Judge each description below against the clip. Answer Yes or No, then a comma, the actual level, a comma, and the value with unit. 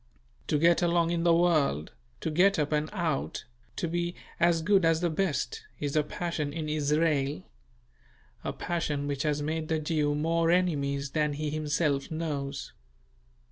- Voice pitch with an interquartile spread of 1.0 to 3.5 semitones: Yes, narrow, 2.5 semitones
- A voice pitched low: No, medium, 155 Hz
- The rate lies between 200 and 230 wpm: No, average, 160 wpm